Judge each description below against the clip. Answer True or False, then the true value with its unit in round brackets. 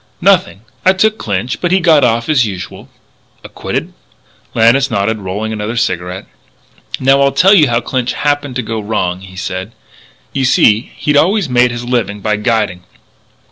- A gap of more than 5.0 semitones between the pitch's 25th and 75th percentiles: True (5.4 semitones)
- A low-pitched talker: True (120 Hz)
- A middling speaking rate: True (165 wpm)